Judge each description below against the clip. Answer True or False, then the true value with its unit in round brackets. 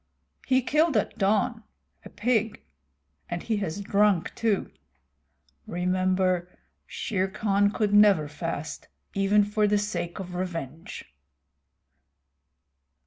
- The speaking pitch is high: True (200 Hz)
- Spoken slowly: True (105 wpm)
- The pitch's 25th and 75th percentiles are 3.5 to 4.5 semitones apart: False (2.8 semitones)